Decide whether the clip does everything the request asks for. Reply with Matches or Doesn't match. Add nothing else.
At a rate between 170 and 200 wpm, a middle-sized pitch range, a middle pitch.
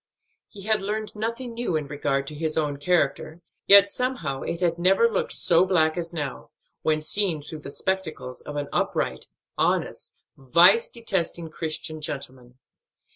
Doesn't match